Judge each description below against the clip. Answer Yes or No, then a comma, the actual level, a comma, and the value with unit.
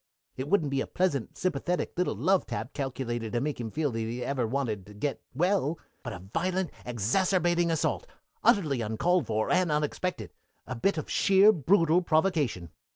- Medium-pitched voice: Yes, medium, 150 Hz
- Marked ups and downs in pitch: Yes, wide, 6.9 semitones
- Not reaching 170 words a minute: No, average, 175 wpm